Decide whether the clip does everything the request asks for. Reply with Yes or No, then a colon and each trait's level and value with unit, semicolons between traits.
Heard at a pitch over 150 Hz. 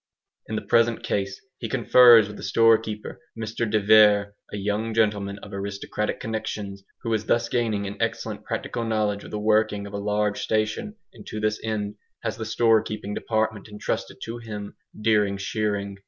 No: low, 105 Hz